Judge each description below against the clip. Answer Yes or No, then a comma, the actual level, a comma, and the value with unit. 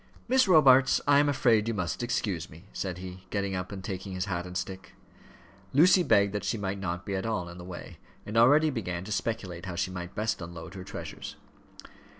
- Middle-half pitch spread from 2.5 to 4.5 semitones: Yes, average, 4.1 semitones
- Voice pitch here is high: No, low, 100 Hz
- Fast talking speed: Yes, fast, 210 wpm